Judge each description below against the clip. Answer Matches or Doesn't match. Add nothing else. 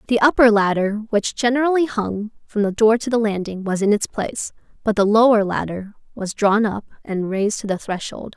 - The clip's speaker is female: Matches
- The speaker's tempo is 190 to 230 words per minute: Matches